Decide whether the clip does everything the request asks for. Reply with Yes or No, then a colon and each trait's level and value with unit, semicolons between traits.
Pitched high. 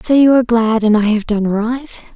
Yes: high, 230 Hz